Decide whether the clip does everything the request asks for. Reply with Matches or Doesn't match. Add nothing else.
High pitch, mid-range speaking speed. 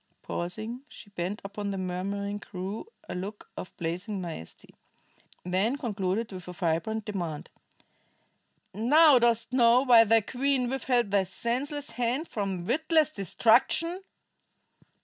Doesn't match